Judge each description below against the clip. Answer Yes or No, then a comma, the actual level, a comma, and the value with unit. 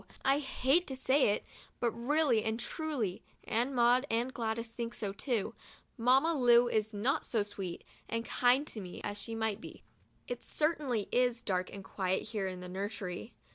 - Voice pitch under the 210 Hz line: No, high, 230 Hz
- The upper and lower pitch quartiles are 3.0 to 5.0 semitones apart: Yes, average, 4.0 semitones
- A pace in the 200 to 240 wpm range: No, average, 175 wpm